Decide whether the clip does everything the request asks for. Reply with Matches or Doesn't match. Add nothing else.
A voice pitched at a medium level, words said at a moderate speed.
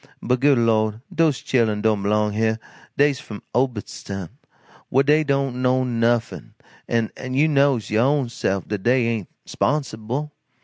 Doesn't match